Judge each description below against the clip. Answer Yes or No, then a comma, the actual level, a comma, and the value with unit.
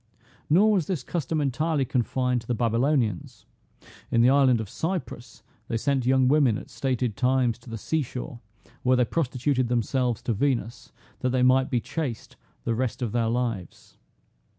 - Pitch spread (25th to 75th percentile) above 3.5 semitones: No, average, 2.8 semitones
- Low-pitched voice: Yes, low, 125 Hz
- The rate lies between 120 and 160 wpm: No, average, 170 wpm